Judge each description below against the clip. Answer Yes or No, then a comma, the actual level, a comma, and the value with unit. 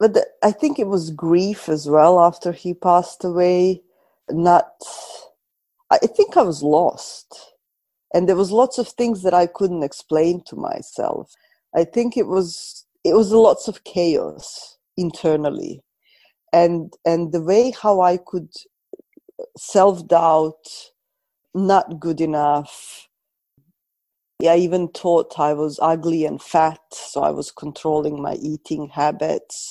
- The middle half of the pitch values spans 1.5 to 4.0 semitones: No, average, 4.6 semitones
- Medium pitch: Yes, medium, 175 Hz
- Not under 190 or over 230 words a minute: No, slow, 135 wpm